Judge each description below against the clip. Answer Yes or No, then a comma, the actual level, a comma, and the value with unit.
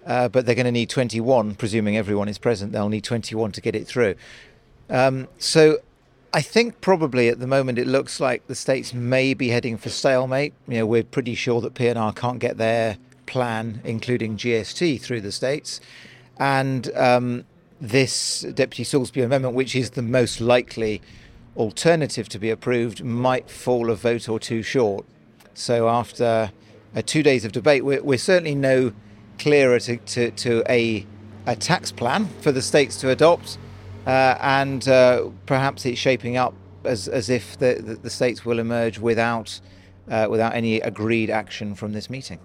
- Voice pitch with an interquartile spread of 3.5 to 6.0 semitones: No, average, 2.7 semitones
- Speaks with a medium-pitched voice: No, low, 120 Hz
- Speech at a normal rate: Yes, average, 170 wpm